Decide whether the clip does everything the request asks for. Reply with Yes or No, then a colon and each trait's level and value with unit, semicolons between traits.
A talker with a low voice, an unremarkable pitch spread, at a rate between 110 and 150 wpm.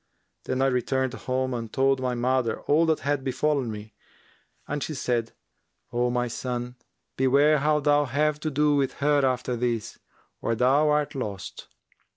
No: low, 130 Hz; average, 3.0 semitones; average, 165 wpm